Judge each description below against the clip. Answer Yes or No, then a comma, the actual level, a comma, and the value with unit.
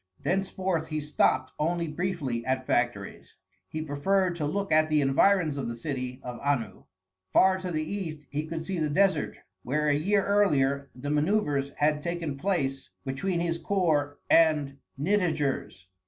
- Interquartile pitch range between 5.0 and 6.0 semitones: No, average, 4.2 semitones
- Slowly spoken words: No, average, 155 wpm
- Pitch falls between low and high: Yes, medium, 155 Hz